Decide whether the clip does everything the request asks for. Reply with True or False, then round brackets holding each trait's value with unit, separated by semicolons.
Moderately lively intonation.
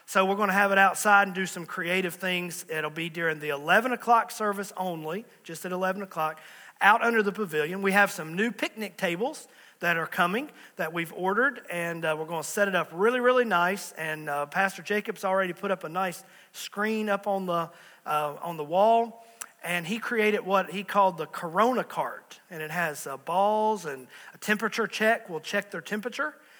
True (3.8 semitones)